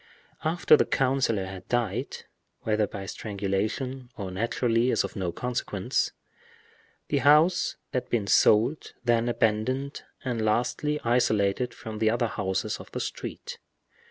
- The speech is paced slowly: Yes, slow, 125 wpm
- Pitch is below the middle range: Yes, low, 115 Hz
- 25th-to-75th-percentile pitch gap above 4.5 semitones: No, average, 3.5 semitones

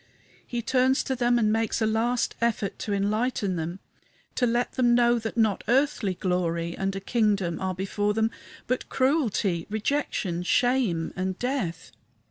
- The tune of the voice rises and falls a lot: No, average, 4.3 semitones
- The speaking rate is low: No, average, 155 wpm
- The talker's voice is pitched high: Yes, high, 220 Hz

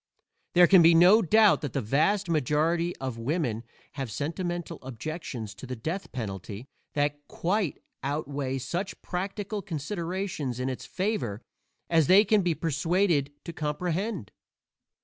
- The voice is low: No, medium, 160 Hz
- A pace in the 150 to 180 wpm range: No, slow, 135 wpm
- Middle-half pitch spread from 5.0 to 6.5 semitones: Yes, wide, 5.4 semitones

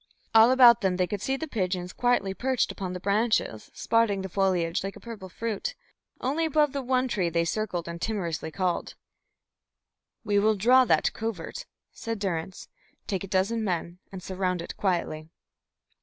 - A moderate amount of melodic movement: Yes, average, 4.2 semitones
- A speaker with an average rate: Yes, average, 170 wpm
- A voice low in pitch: No, high, 200 Hz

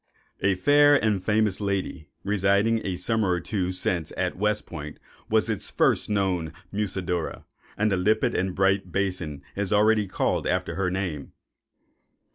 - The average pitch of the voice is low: Yes, very low, 95 Hz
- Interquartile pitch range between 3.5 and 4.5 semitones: No, average, 2.7 semitones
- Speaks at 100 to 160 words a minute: Yes, average, 150 wpm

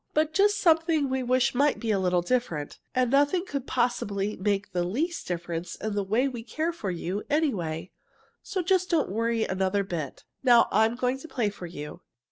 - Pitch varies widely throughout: Yes, wide, 7.2 semitones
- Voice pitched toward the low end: No, high, 235 Hz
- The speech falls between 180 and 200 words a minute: Yes, average, 190 wpm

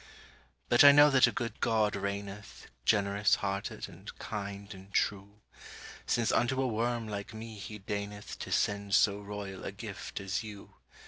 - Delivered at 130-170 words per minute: Yes, average, 165 wpm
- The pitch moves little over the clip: Yes, narrow, 2.0 semitones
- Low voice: Yes, low, 105 Hz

